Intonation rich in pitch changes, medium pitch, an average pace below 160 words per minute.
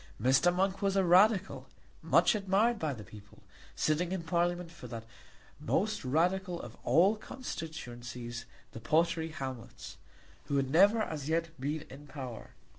Yes: wide, 6.1 semitones; medium, 160 Hz; average, 145 wpm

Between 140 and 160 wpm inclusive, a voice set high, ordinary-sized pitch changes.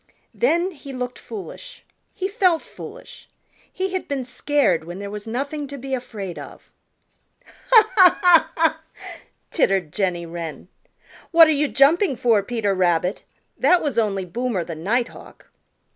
No: average, 145 wpm; very high, 255 Hz; wide, 9.0 semitones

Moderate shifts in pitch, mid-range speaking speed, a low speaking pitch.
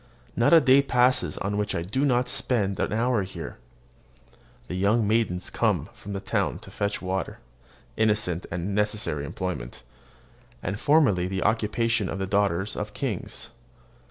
Yes: average, 3.7 semitones; average, 155 wpm; low, 105 Hz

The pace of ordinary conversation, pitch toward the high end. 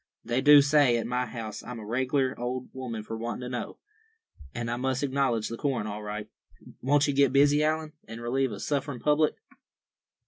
No: average, 195 wpm; low, 130 Hz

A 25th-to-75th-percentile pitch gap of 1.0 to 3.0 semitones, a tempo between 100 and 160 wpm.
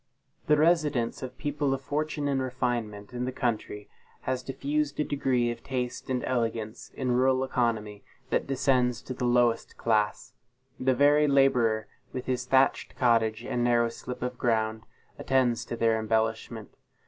Yes: narrow, 2.6 semitones; average, 155 wpm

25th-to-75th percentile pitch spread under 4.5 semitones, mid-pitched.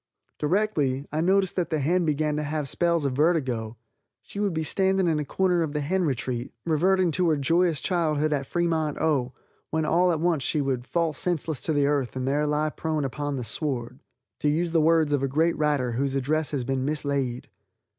Yes: average, 3.4 semitones; medium, 150 Hz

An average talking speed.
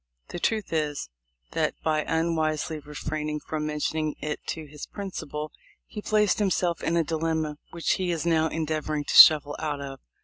Yes: average, 165 wpm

